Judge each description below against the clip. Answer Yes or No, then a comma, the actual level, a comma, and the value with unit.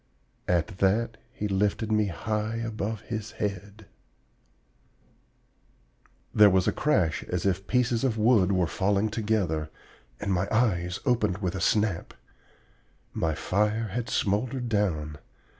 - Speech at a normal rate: No, slow, 130 wpm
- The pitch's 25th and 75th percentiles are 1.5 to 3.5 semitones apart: Yes, average, 3.2 semitones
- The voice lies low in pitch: Yes, low, 105 Hz